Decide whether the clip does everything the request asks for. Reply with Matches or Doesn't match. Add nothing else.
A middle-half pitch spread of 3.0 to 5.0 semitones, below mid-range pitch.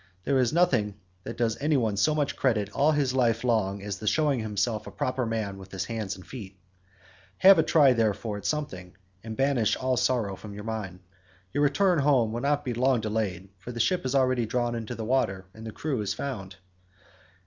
Matches